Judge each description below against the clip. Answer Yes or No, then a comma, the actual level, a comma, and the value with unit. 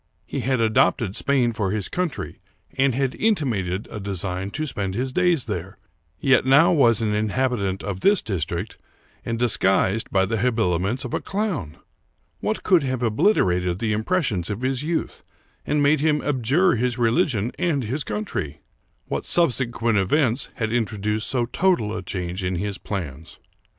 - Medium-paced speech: Yes, average, 160 wpm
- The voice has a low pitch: Yes, low, 115 Hz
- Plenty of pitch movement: Yes, wide, 5.7 semitones